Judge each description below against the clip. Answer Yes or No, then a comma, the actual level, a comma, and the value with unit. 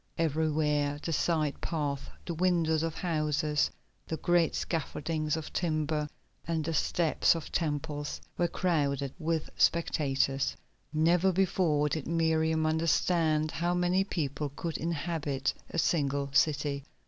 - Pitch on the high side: No, medium, 155 Hz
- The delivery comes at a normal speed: No, slow, 125 wpm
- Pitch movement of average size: No, narrow, 2.1 semitones